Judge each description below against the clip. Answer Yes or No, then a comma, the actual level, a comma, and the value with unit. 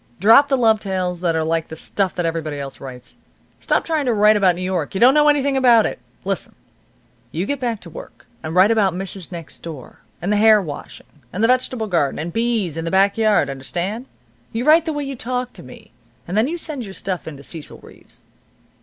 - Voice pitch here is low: No, high, 200 Hz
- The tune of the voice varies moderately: No, wide, 6.2 semitones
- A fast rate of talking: Yes, fast, 225 wpm